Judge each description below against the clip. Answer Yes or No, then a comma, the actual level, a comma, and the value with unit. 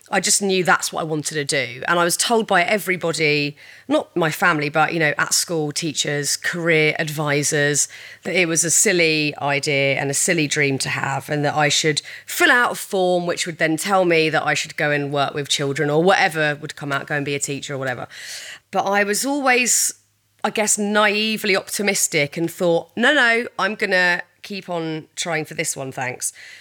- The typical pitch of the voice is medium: Yes, medium, 165 Hz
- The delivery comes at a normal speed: No, fast, 210 wpm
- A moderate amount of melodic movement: Yes, average, 4.6 semitones